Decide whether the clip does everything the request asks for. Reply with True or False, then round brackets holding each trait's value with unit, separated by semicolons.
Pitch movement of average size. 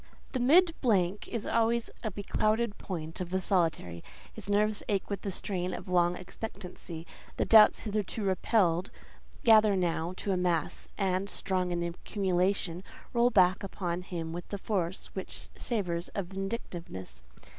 True (3.1 semitones)